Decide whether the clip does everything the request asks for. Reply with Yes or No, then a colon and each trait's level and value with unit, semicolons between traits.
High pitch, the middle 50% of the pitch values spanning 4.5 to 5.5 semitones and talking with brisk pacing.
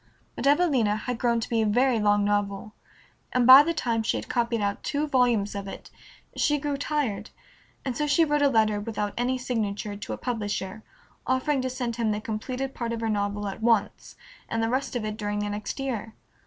No: high, 230 Hz; average, 3.8 semitones; fast, 210 wpm